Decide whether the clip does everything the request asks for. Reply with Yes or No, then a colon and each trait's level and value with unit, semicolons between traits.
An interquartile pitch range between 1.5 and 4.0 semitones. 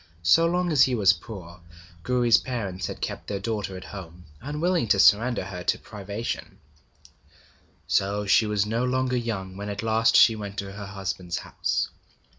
Yes: average, 3.7 semitones